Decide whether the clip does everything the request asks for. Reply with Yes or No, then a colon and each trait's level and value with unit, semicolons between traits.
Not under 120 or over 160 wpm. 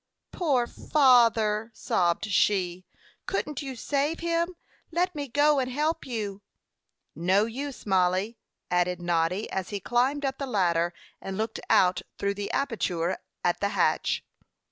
Yes: average, 140 wpm